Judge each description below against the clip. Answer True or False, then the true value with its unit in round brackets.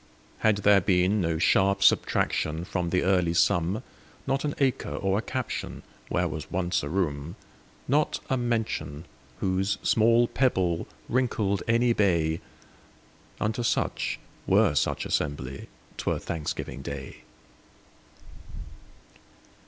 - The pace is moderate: False (100 wpm)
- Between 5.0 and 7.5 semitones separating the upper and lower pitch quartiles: True (5.3 semitones)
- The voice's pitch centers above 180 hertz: False (95 Hz)